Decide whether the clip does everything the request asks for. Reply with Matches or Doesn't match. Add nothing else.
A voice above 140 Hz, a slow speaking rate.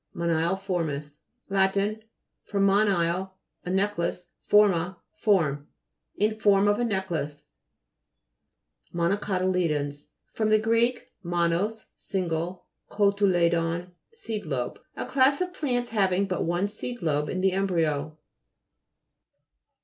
Matches